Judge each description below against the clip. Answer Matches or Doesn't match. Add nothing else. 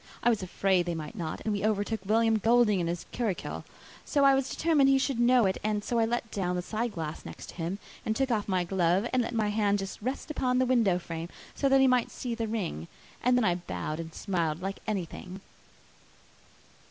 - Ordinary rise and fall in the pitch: Matches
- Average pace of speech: Doesn't match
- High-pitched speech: Matches